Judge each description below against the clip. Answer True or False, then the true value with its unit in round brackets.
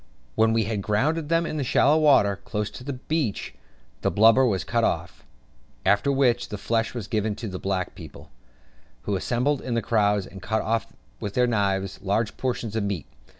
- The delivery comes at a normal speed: True (195 wpm)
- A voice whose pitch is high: False (110 Hz)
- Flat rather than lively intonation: False (3.7 semitones)